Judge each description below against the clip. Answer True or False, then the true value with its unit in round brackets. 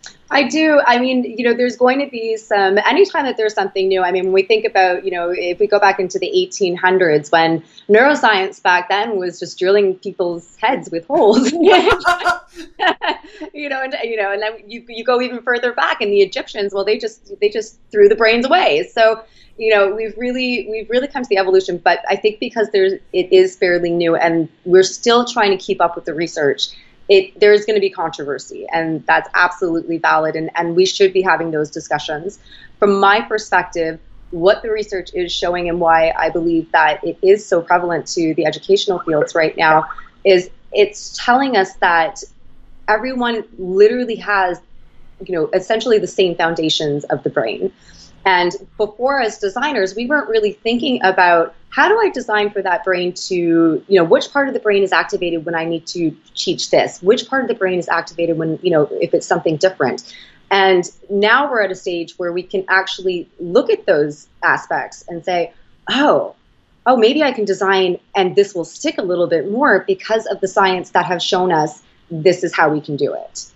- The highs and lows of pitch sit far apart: True (5.8 semitones)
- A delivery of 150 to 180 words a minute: False (200 wpm)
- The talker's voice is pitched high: True (195 Hz)